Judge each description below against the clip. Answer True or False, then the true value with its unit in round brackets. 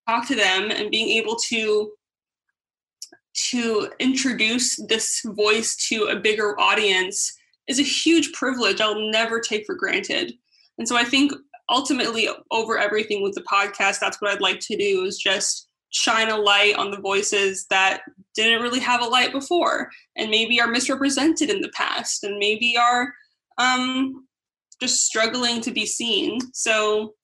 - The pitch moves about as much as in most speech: True (3.9 semitones)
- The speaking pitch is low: False (230 Hz)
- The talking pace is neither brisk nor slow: True (160 wpm)